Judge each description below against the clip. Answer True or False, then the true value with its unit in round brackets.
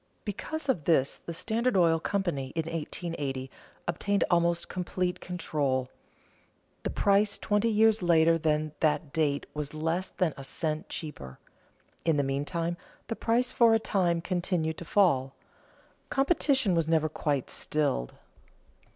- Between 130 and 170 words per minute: True (135 wpm)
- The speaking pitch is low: False (170 Hz)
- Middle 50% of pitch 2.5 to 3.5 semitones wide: False (4.5 semitones)